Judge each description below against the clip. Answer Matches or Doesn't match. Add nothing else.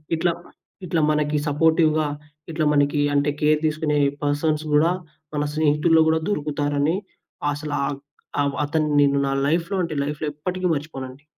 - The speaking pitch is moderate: Matches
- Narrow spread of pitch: Matches